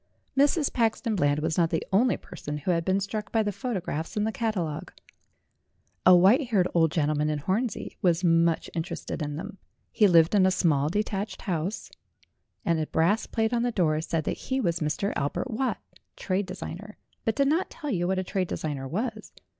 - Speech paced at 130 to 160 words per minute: No, average, 195 wpm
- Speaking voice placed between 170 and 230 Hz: Yes, medium, 185 Hz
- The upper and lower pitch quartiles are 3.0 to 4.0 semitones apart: No, average, 5.2 semitones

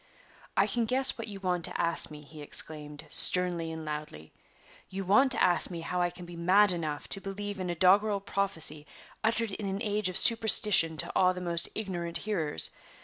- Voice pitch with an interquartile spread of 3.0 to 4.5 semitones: Yes, average, 3.7 semitones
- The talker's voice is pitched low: No, medium, 180 Hz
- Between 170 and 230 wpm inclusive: Yes, average, 200 wpm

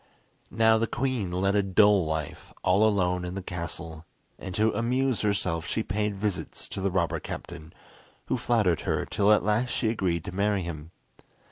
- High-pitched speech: No, low, 100 Hz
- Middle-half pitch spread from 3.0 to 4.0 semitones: Yes, average, 3.3 semitones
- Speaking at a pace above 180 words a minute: No, average, 175 wpm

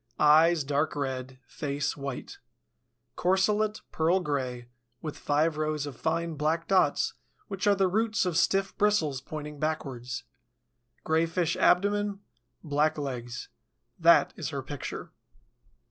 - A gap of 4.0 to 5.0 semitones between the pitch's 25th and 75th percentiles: Yes, average, 4.4 semitones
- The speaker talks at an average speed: No, slow, 120 wpm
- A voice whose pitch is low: No, medium, 155 Hz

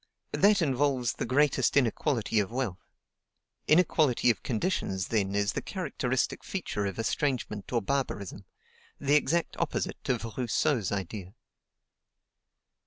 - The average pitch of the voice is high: No, low, 125 Hz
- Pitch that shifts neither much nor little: No, wide, 5.8 semitones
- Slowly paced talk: Yes, slow, 115 wpm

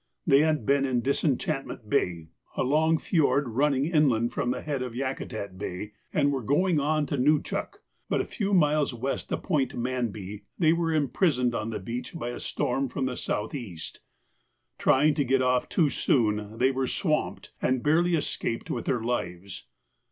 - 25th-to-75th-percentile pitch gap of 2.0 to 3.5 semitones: No, average, 4.3 semitones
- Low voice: Yes, low, 130 Hz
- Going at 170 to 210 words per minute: Yes, average, 180 wpm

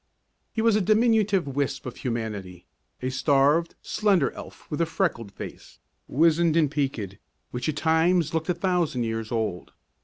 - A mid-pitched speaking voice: Yes, medium, 150 Hz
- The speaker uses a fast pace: No, average, 155 wpm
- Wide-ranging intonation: Yes, wide, 5.9 semitones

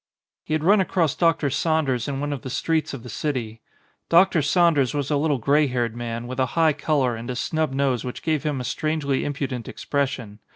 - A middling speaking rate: No, fast, 215 wpm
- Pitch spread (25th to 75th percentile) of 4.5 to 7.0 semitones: No, average, 3.8 semitones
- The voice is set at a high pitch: No, medium, 140 Hz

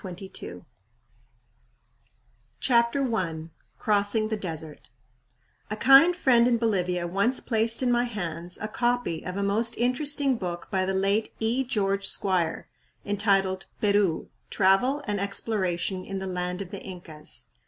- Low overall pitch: No, high, 200 Hz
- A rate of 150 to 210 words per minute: No, average, 140 wpm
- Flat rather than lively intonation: No, average, 4.2 semitones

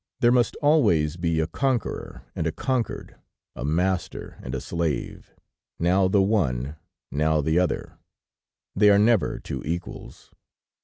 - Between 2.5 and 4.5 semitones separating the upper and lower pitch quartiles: No, average, 5.2 semitones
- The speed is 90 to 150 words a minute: Yes, average, 140 wpm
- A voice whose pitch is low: Yes, very low, 90 Hz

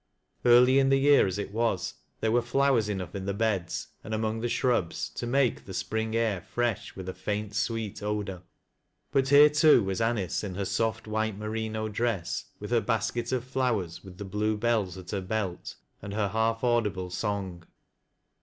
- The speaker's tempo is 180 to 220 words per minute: Yes, average, 185 wpm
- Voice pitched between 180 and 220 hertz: No, low, 110 Hz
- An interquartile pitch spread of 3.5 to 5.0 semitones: No, average, 3.1 semitones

